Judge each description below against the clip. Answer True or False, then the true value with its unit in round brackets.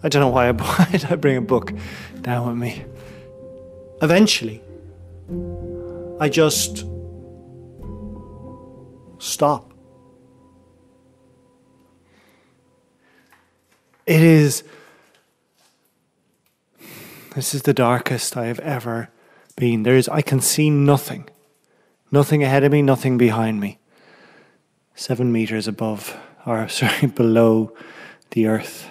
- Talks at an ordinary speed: False (95 wpm)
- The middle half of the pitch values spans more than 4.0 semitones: True (5.1 semitones)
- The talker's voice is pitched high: False (120 Hz)